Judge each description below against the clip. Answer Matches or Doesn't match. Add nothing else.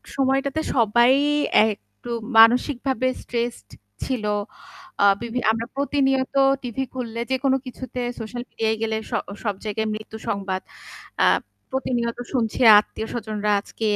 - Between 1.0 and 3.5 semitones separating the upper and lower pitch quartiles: Matches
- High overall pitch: Matches